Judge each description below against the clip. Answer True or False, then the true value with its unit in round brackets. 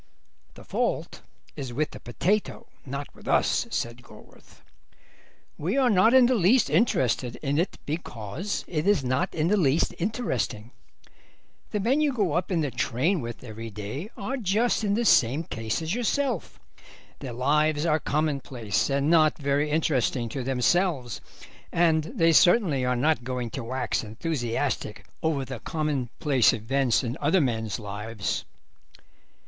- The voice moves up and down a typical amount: False (6.1 semitones)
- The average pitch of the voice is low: False (145 Hz)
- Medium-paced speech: True (150 wpm)